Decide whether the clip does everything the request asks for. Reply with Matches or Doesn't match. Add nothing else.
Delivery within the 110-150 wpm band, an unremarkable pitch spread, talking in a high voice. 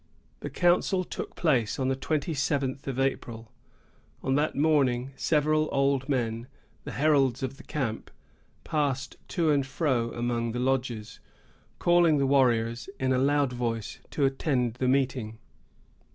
Doesn't match